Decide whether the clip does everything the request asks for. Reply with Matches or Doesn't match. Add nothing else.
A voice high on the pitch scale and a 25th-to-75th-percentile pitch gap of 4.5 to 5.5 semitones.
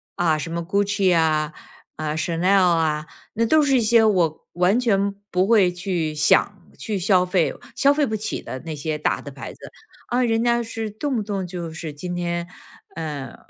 Doesn't match